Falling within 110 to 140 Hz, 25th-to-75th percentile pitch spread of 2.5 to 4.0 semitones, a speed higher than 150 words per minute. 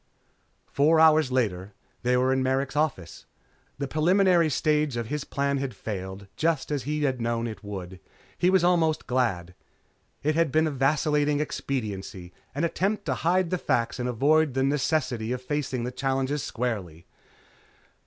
No: low, 135 Hz; average, 4.6 semitones; average, 160 wpm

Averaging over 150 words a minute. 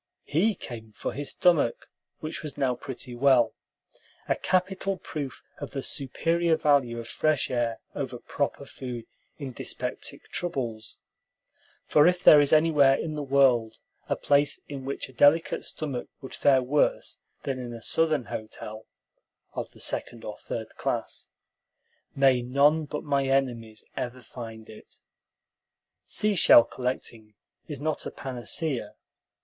No: average, 140 wpm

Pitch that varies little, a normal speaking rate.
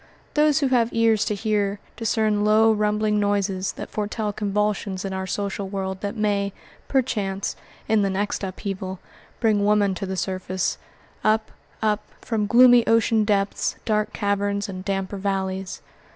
Yes: narrow, 1.8 semitones; average, 150 wpm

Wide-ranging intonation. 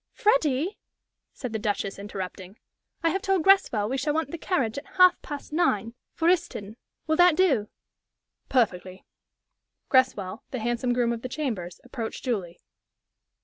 Yes: wide, 7.4 semitones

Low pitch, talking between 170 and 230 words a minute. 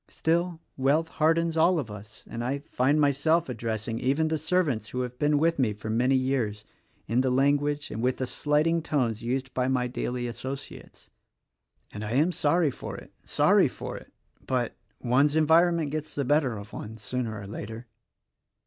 Yes: low, 130 Hz; average, 180 wpm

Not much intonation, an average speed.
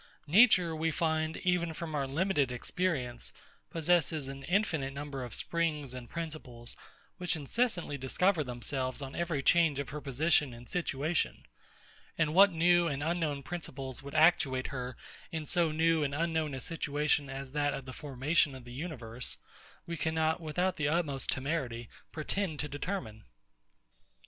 No: average, 3.8 semitones; average, 150 wpm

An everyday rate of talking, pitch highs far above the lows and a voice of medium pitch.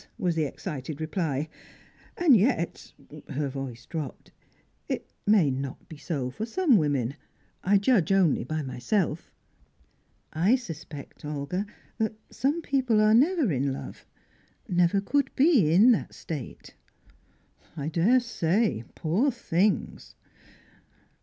No: slow, 120 wpm; wide, 7.4 semitones; medium, 175 Hz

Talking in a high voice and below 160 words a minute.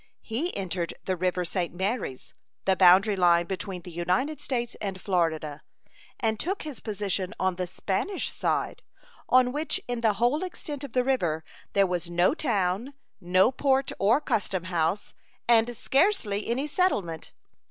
Yes: high, 200 Hz; average, 150 wpm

